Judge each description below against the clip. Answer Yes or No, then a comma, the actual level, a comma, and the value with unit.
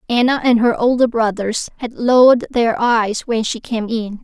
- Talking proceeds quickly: No, average, 185 wpm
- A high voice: Yes, high, 230 Hz